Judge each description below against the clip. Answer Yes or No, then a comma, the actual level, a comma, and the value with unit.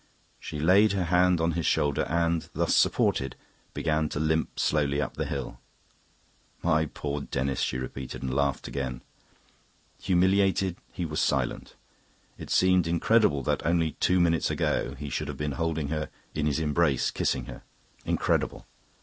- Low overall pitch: Yes, very low, 80 Hz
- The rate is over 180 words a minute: No, average, 155 wpm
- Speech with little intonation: No, average, 3.3 semitones